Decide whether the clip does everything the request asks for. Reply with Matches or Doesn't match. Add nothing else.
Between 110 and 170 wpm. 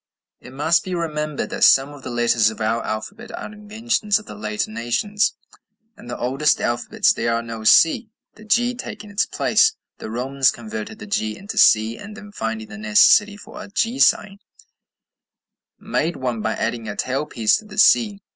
Doesn't match